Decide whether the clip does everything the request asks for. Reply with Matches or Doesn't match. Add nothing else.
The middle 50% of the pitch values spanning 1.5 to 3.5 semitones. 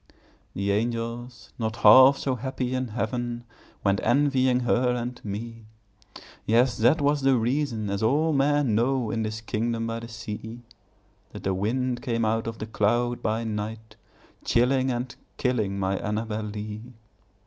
Matches